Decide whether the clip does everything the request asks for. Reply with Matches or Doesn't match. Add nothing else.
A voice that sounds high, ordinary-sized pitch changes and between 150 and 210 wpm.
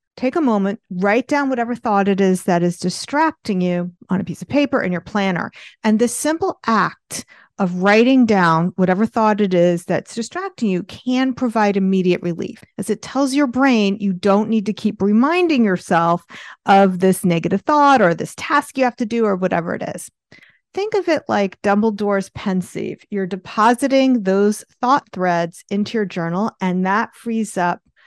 Matches